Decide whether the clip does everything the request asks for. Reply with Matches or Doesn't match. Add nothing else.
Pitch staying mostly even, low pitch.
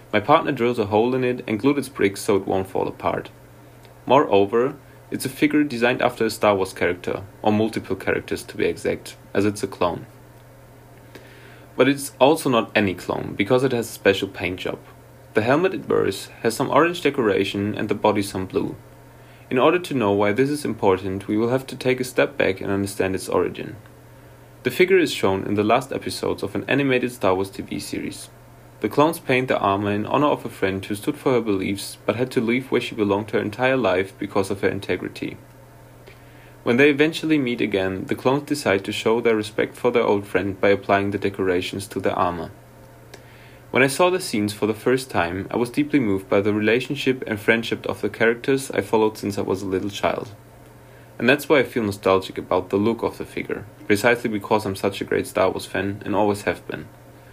Doesn't match